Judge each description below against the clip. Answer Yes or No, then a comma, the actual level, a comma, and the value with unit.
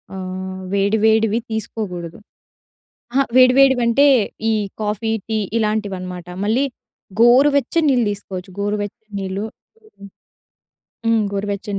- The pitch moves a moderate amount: Yes, average, 3.0 semitones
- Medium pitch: No, high, 215 Hz